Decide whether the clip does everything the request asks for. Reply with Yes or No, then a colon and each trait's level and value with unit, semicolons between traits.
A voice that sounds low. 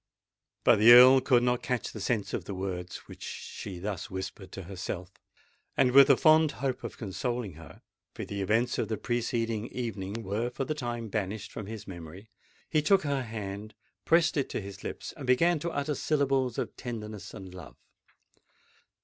Yes: low, 115 Hz